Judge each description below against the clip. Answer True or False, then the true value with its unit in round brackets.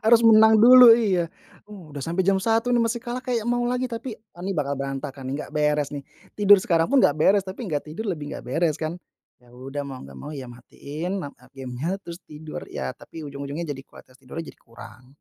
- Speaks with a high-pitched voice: False (165 Hz)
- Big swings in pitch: True (7.6 semitones)